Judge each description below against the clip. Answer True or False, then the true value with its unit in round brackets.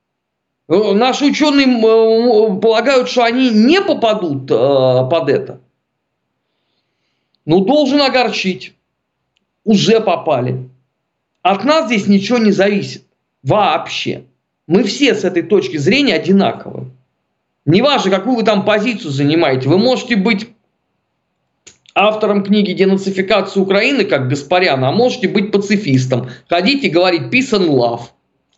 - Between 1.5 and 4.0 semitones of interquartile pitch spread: False (5.2 semitones)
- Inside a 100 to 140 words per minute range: True (110 wpm)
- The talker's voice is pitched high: True (200 Hz)